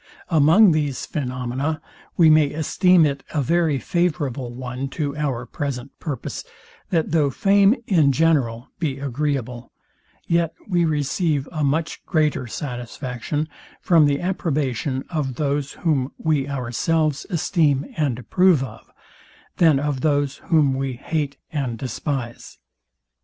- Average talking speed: No, slow, 125 wpm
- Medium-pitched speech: Yes, medium, 145 Hz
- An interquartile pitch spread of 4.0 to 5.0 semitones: No, average, 3.3 semitones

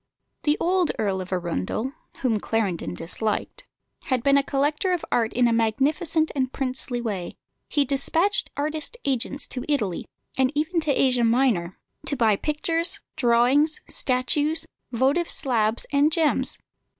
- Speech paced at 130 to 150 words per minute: Yes, average, 140 wpm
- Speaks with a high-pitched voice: Yes, very high, 265 Hz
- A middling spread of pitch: Yes, average, 4.8 semitones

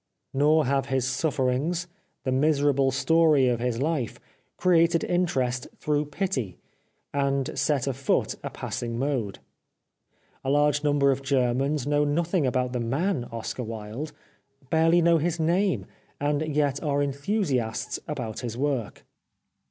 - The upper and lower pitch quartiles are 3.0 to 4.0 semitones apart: Yes, average, 3.5 semitones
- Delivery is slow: Yes, slow, 130 wpm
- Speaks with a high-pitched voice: No, medium, 140 Hz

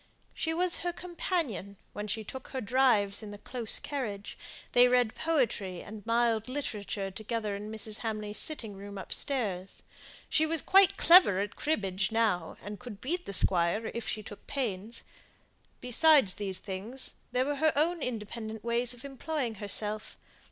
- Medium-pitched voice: No, high, 225 Hz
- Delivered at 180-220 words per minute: No, average, 160 wpm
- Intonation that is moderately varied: Yes, average, 4.7 semitones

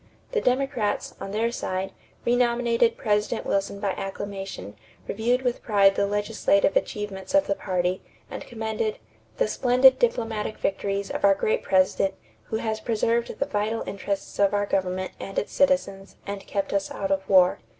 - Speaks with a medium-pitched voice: No, high, 205 Hz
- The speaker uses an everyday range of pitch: Yes, average, 3.0 semitones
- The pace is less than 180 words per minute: Yes, average, 160 wpm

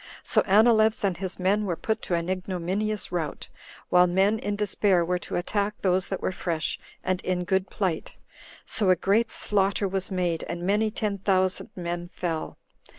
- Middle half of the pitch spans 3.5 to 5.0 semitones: No, narrow, 2.5 semitones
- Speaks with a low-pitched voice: No, high, 190 Hz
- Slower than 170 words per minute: No, average, 175 wpm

